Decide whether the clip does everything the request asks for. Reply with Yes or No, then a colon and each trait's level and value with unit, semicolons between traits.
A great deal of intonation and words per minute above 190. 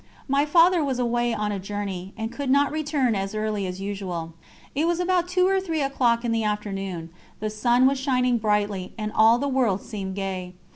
Yes: wide, 5.7 semitones; average, 200 wpm